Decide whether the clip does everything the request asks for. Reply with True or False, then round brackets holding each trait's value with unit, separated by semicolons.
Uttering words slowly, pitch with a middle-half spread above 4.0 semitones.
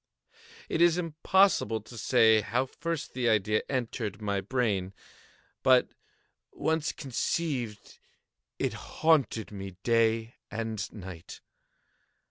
True (100 wpm; 4.5 semitones)